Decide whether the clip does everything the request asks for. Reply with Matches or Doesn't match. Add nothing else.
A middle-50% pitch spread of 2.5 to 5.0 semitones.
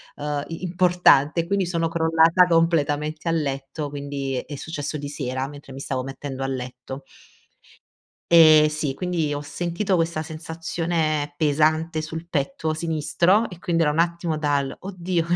Matches